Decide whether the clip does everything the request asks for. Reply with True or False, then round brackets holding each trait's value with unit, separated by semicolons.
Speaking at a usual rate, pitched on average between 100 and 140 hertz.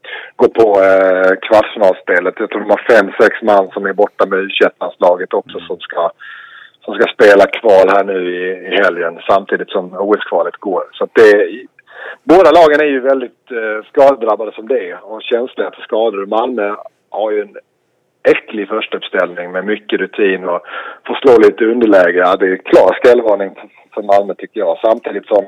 True (185 wpm; 135 Hz)